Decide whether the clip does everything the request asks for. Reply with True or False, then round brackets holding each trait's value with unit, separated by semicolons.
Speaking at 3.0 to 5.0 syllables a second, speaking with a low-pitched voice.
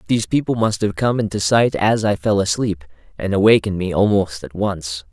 False (5.5 syllables/s; 100 Hz)